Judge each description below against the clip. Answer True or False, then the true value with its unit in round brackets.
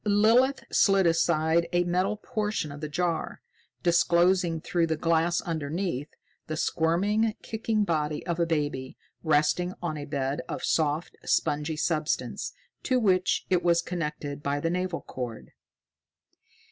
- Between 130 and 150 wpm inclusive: True (135 wpm)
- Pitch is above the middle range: False (170 Hz)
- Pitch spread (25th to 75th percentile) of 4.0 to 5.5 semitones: False (3.2 semitones)